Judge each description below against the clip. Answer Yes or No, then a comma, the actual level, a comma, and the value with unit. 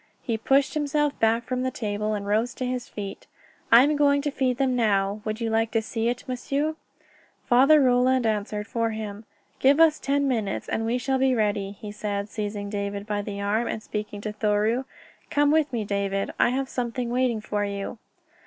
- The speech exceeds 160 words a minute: Yes, average, 200 wpm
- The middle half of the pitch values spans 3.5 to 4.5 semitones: Yes, average, 3.8 semitones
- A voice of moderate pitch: No, high, 225 Hz